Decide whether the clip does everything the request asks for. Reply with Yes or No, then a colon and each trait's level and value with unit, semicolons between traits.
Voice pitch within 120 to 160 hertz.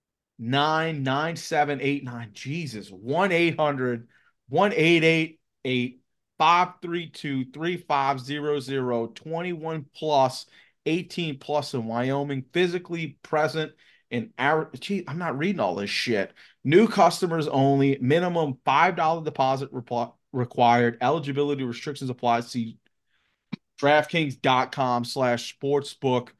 Yes: medium, 140 Hz